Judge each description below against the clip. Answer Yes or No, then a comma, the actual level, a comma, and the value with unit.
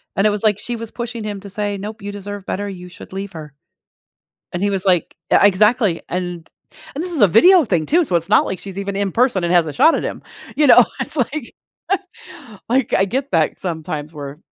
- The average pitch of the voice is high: Yes, high, 200 Hz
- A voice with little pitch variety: No, average, 4.2 semitones